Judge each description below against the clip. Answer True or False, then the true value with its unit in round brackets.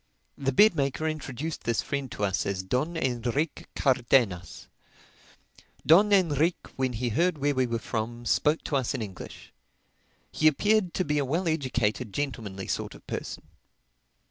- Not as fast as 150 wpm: False (155 wpm)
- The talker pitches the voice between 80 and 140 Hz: True (135 Hz)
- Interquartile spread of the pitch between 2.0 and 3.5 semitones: False (5.0 semitones)